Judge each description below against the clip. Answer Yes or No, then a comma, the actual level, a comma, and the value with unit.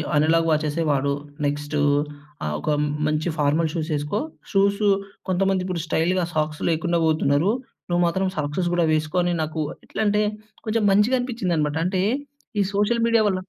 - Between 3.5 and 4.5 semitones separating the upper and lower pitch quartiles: Yes, average, 4.1 semitones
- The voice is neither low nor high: Yes, medium, 170 Hz